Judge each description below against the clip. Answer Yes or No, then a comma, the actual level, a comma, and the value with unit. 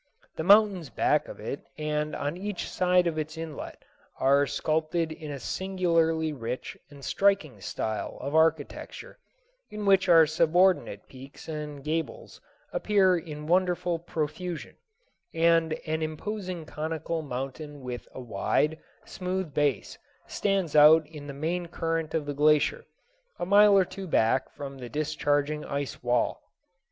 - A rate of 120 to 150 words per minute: Yes, average, 140 wpm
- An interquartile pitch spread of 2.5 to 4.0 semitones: Yes, average, 3.5 semitones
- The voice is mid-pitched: Yes, medium, 155 Hz